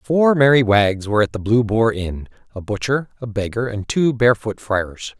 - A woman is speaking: No, male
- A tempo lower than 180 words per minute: No, average, 195 wpm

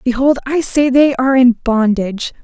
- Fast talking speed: No, average, 175 wpm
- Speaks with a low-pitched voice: No, very high, 255 Hz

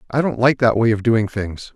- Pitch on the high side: No, low, 115 Hz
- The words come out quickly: Yes, fast, 275 wpm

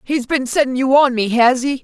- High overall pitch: Yes, very high, 260 Hz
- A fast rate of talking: Yes, fast, 260 wpm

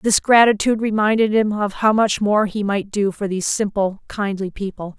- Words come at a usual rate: Yes, average, 195 wpm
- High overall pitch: Yes, high, 205 Hz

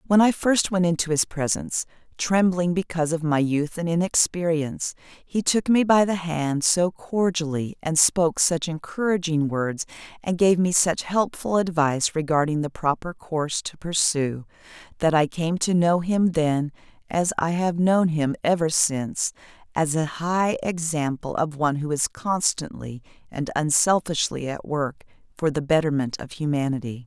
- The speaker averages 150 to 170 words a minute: Yes, average, 155 wpm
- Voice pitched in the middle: Yes, medium, 165 Hz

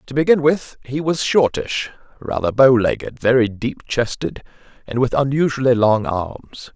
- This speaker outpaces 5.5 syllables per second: No, 4.5 syllables/s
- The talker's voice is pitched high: No, low, 125 Hz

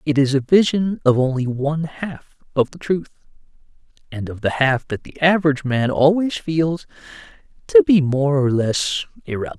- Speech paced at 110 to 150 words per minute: No, average, 170 wpm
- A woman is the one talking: No, male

